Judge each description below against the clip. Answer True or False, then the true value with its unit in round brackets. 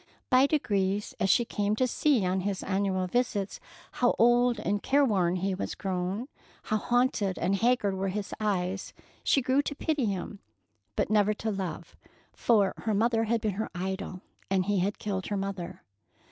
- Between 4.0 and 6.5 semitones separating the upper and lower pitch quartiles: False (3.5 semitones)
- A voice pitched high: True (205 Hz)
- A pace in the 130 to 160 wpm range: False (175 wpm)